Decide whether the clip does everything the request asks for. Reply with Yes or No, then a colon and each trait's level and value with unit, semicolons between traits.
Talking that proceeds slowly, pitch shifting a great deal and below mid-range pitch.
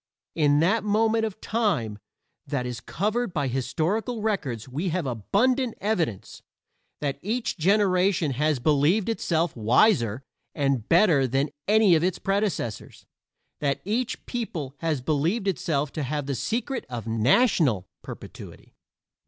No: slow, 130 wpm; wide, 7.7 semitones; medium, 165 Hz